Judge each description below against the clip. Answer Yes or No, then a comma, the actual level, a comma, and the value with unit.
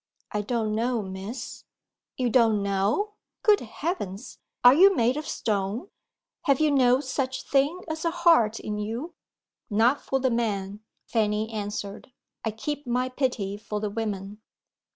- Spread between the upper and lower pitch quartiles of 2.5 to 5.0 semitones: Yes, average, 4.6 semitones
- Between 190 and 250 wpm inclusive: No, average, 150 wpm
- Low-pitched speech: No, high, 235 Hz